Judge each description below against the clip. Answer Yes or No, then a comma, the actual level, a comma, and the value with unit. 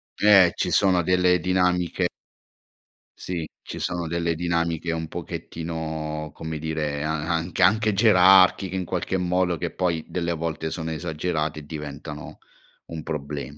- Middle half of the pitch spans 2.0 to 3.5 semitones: Yes, narrow, 2.4 semitones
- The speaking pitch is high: No, very low, 85 Hz